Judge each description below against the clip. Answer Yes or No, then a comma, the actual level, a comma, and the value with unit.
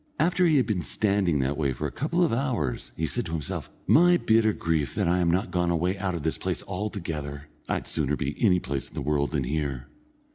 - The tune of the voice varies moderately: No, wide, 6.5 semitones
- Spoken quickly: Yes, fast, 230 wpm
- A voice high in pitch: No, very low, 85 Hz